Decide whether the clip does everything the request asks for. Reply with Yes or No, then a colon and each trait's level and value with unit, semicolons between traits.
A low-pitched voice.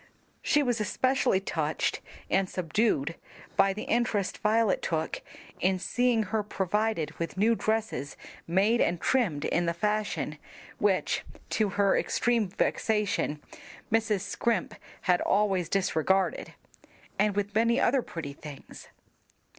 No: high, 200 Hz